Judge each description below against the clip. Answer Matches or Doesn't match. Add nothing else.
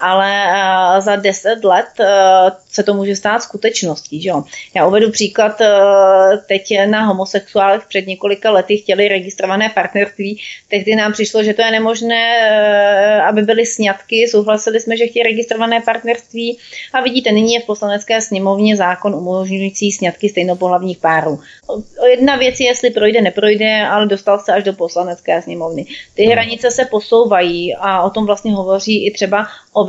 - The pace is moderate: Matches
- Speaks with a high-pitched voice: Matches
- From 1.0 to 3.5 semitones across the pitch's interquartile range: Matches